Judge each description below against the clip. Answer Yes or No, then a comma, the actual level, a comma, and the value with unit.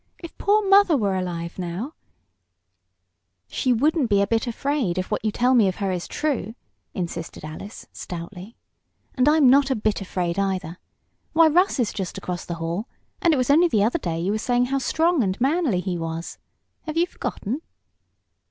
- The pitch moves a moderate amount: No, wide, 7.9 semitones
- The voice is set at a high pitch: Yes, high, 215 Hz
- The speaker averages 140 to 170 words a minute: No, average, 190 wpm